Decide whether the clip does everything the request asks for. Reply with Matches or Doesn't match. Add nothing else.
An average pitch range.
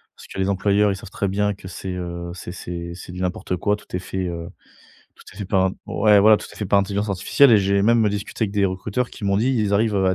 Doesn't match